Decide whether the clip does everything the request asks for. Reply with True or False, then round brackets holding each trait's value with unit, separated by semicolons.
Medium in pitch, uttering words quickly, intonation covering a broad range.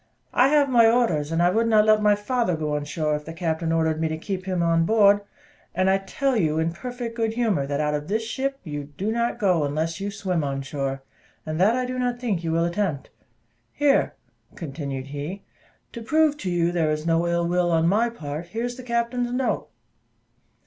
True (180 Hz; 220 wpm; 6.4 semitones)